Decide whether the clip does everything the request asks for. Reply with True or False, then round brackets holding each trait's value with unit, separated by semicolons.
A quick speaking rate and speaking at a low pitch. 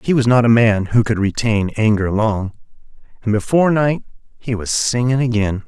False (180 wpm; 115 Hz)